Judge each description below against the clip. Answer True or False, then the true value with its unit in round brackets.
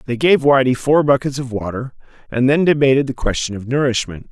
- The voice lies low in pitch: True (130 Hz)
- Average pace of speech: True (195 wpm)